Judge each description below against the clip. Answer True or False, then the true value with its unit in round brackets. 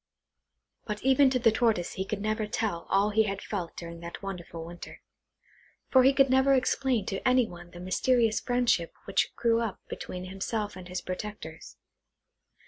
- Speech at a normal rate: True (170 wpm)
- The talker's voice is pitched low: False (210 Hz)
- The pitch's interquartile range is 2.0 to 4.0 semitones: False (5.1 semitones)